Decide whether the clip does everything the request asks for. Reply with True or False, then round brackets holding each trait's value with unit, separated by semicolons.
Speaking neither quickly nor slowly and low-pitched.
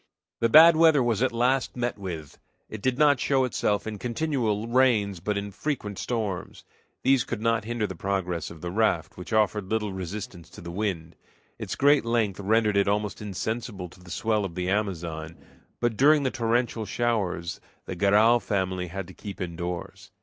True (180 wpm; 105 Hz)